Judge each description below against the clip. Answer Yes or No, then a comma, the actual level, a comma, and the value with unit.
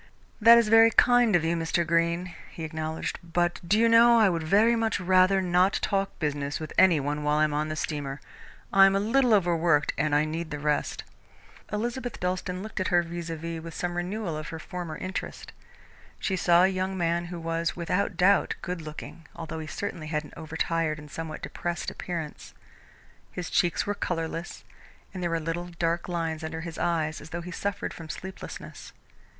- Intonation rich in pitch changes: No, average, 2.9 semitones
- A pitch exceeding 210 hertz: No, medium, 170 Hz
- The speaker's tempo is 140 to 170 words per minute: No, average, 200 wpm